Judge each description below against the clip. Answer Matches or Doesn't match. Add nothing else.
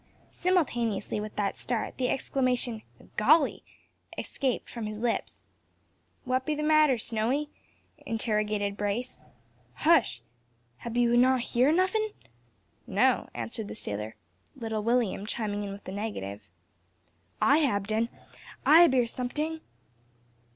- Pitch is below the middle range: Doesn't match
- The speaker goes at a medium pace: Doesn't match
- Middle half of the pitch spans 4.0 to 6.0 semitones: Matches